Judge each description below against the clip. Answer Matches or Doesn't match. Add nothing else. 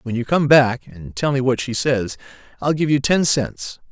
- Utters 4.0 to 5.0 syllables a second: Matches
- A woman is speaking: Doesn't match